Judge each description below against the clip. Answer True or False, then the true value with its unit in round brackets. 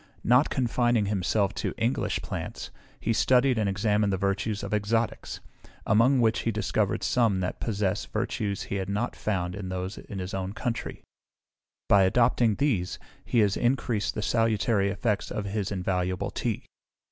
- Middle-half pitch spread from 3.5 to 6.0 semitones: False (2.9 semitones)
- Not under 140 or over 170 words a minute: True (160 wpm)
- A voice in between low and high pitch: False (105 Hz)